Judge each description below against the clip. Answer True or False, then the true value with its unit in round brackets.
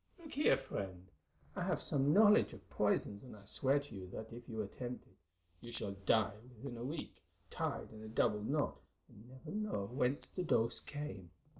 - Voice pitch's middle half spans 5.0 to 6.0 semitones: True (5.6 semitones)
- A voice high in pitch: False (120 Hz)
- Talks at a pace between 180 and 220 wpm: True (190 wpm)